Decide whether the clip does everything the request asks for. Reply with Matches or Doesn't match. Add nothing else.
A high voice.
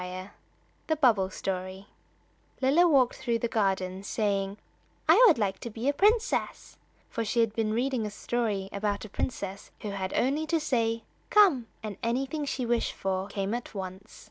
Matches